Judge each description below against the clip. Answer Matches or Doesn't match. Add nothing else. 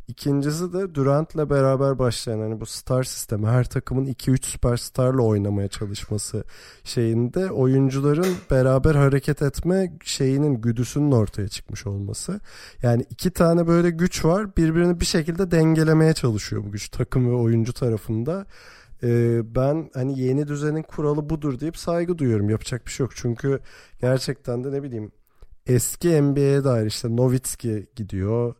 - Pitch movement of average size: Matches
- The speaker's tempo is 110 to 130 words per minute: Doesn't match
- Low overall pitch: Matches